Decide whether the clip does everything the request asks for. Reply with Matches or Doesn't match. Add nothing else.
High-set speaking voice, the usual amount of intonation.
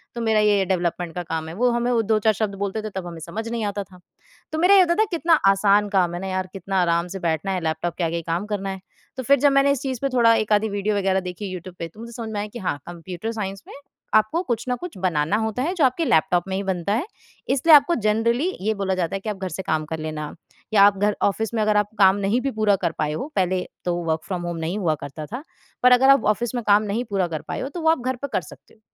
Matches